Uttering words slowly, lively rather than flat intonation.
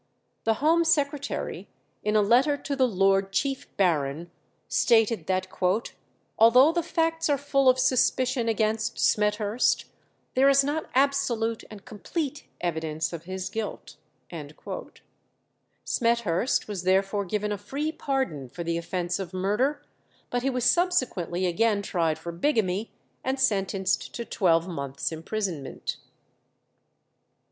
Yes: slow, 125 wpm; wide, 6.4 semitones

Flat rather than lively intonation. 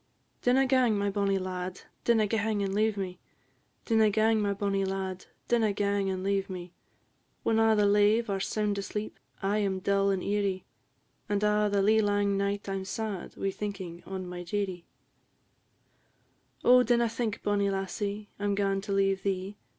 Yes: narrow, 1.5 semitones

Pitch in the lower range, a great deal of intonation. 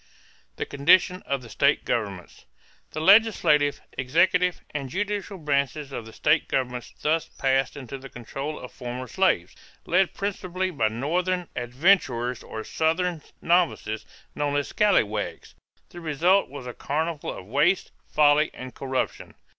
No: medium, 145 Hz; wide, 5.7 semitones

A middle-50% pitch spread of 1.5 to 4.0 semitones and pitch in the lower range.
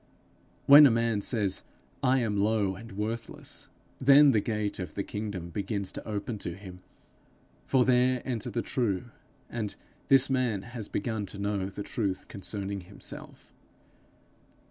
Yes: average, 3.3 semitones; low, 105 Hz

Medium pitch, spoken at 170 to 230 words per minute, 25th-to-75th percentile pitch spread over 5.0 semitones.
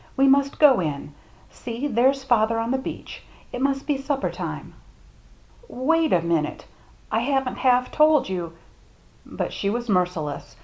No: very high, 250 Hz; average, 175 wpm; wide, 5.6 semitones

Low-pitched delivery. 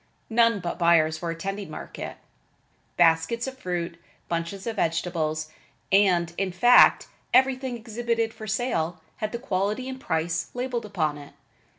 No: high, 195 Hz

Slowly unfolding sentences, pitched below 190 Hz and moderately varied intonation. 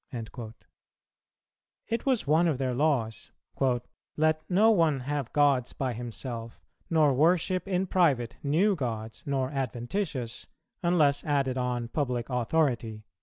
Yes: slow, 125 wpm; medium, 140 Hz; average, 4.9 semitones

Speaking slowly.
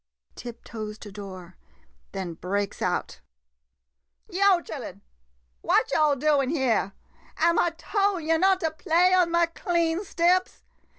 Yes: slow, 130 wpm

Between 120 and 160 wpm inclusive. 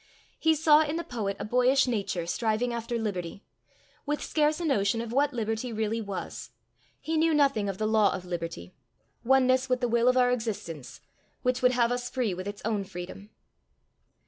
No: average, 185 wpm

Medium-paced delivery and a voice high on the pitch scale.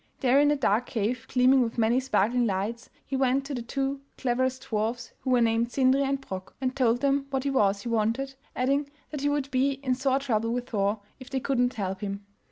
No: fast, 225 wpm; very high, 250 Hz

